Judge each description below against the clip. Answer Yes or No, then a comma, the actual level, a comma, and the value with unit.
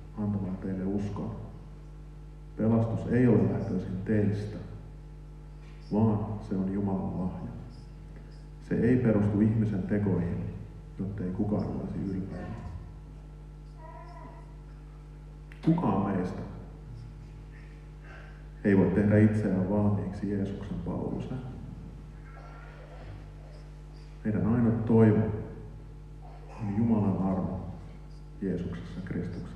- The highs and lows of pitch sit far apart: Yes, wide, 7.5 semitones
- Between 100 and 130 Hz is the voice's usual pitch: Yes, low, 110 Hz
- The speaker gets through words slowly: Yes, slow, 80 wpm